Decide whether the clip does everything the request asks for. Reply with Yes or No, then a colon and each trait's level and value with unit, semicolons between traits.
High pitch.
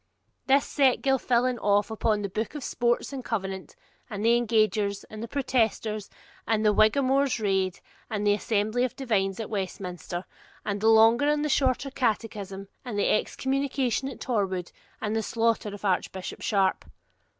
Yes: high, 220 Hz